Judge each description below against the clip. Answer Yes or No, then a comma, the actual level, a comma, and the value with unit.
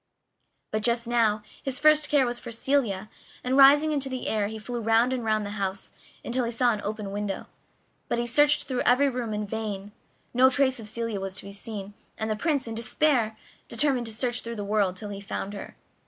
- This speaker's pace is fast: Yes, fast, 215 wpm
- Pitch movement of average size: Yes, average, 3.6 semitones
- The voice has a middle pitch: No, high, 230 Hz